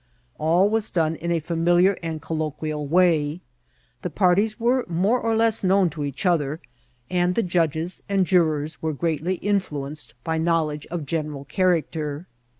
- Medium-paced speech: Yes, average, 150 wpm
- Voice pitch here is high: No, medium, 170 Hz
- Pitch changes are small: No, average, 3.1 semitones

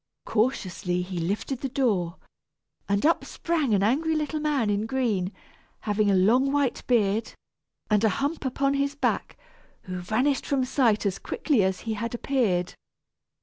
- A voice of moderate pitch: No, high, 230 Hz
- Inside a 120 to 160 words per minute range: Yes, average, 155 wpm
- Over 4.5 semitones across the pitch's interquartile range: Yes, wide, 5.6 semitones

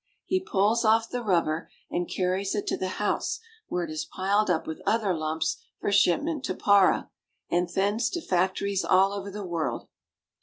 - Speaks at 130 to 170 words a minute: No, average, 180 wpm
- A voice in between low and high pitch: No, high, 195 Hz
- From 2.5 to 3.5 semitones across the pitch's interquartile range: Yes, average, 3.0 semitones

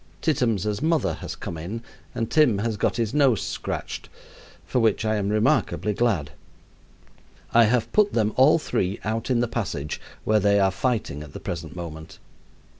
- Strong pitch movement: No, average, 4.0 semitones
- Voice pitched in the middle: No, low, 110 Hz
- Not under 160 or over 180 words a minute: Yes, average, 170 wpm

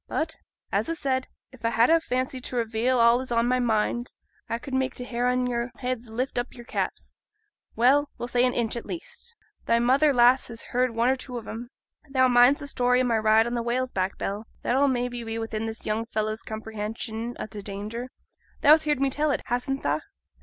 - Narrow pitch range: Yes, narrow, 2.3 semitones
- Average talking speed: No, fast, 225 wpm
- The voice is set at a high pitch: Yes, high, 245 Hz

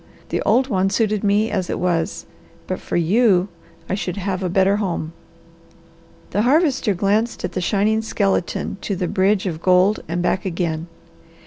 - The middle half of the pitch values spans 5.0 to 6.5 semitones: No, average, 2.9 semitones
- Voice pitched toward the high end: Yes, high, 195 Hz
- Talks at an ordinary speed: Yes, average, 170 wpm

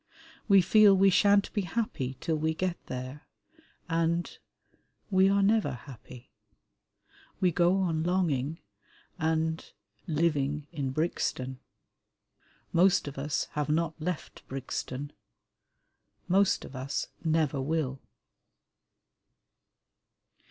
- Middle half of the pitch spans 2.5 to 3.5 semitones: No, average, 4.6 semitones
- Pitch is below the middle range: No, medium, 160 Hz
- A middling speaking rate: No, slow, 100 wpm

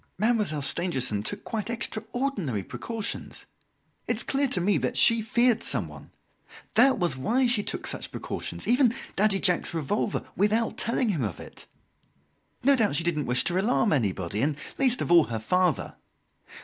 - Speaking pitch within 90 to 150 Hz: No, high, 200 Hz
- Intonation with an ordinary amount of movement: No, wide, 7.8 semitones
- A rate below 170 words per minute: Yes, average, 160 wpm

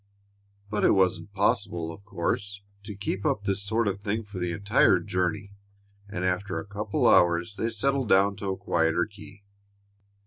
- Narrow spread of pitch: Yes, narrow, 2.1 semitones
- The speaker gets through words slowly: No, average, 175 wpm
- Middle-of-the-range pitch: No, low, 100 Hz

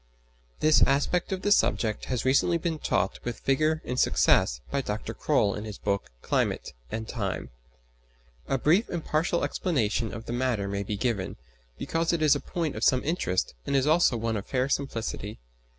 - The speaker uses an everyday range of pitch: No, wide, 6.3 semitones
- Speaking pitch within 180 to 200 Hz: No, low, 130 Hz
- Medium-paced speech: Yes, average, 180 wpm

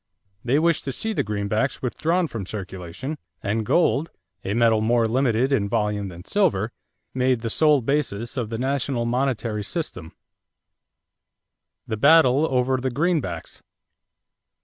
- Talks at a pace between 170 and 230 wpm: No, slow, 135 wpm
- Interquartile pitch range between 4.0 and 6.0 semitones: Yes, average, 4.7 semitones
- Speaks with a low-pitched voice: Yes, low, 120 Hz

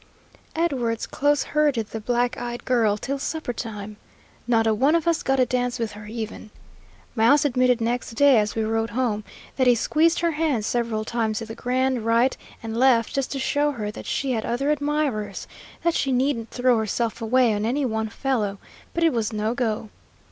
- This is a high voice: Yes, high, 240 Hz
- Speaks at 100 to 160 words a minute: No, average, 195 wpm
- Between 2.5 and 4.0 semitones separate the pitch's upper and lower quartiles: Yes, average, 3.4 semitones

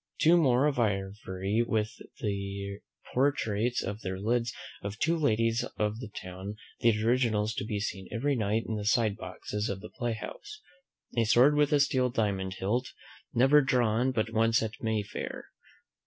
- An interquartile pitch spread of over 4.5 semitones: No, average, 3.4 semitones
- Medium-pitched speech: No, low, 110 Hz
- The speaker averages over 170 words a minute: No, average, 165 wpm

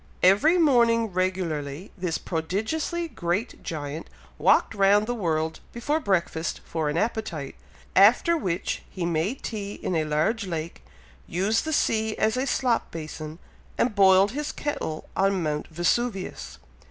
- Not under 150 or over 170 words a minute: No, average, 140 wpm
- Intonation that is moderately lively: No, wide, 6.0 semitones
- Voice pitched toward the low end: No, high, 190 Hz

